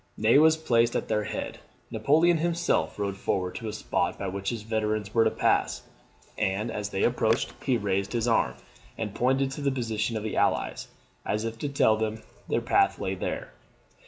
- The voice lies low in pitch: Yes, low, 110 Hz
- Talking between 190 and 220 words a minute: Yes, average, 195 wpm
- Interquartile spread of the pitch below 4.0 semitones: Yes, average, 3.2 semitones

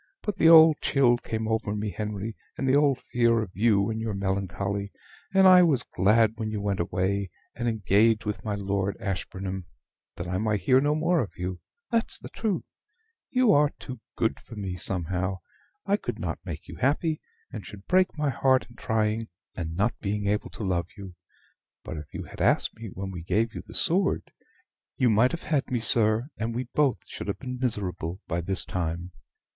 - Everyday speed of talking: Yes, average, 195 wpm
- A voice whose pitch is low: Yes, low, 110 Hz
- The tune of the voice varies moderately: Yes, average, 4.9 semitones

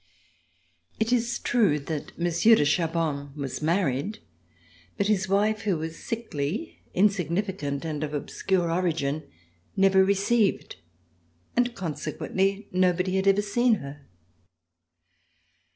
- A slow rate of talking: Yes, slow, 115 wpm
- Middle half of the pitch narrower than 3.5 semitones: No, average, 4.9 semitones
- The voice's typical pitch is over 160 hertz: Yes, medium, 185 Hz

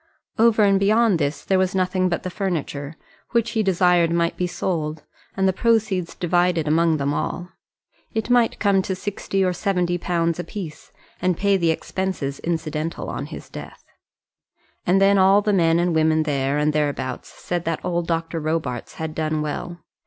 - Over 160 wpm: Yes, average, 175 wpm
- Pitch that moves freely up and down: No, average, 3.3 semitones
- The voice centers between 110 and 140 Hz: No, medium, 175 Hz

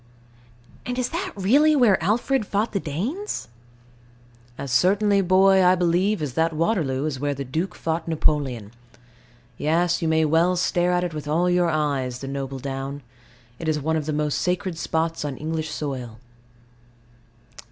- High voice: No, medium, 165 Hz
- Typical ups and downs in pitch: Yes, average, 4.3 semitones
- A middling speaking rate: Yes, average, 165 wpm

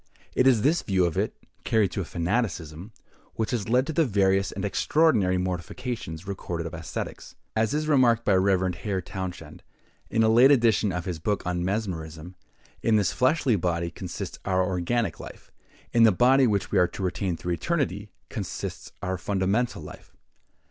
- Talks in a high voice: No, low, 100 Hz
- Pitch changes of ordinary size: Yes, average, 4.6 semitones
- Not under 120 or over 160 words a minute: No, average, 175 wpm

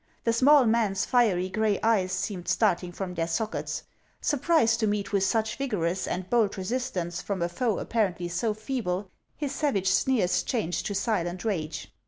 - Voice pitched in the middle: No, high, 205 Hz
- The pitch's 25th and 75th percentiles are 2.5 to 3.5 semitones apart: No, average, 4.2 semitones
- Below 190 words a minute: Yes, average, 170 wpm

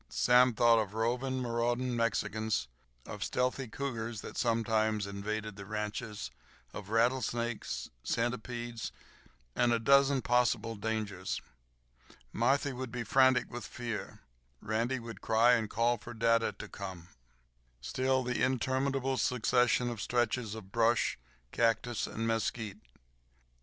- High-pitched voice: No, low, 115 Hz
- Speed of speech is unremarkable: No, slow, 120 wpm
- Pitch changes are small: Yes, narrow, 2.2 semitones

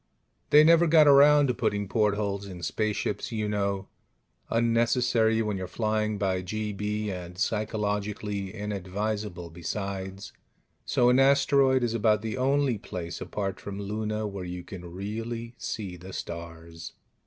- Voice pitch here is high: No, low, 105 Hz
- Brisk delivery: No, slow, 135 wpm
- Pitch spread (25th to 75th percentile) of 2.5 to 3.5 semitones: Yes, average, 3.1 semitones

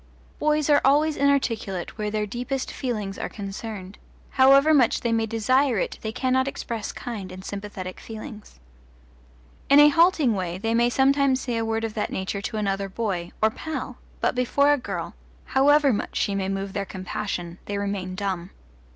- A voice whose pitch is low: No, high, 225 Hz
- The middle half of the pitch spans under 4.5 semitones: No, average, 5.2 semitones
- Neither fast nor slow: Yes, average, 175 wpm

